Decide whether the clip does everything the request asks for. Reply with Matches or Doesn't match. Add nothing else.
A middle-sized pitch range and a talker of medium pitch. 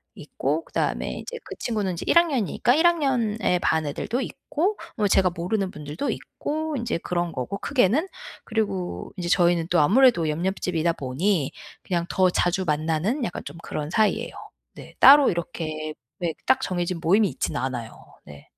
Doesn't match